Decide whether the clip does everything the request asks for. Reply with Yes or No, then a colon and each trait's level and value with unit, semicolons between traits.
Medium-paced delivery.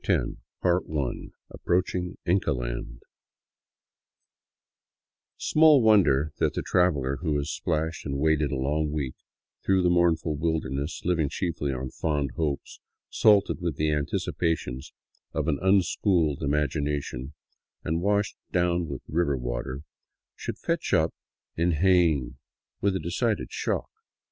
No: slow, 130 wpm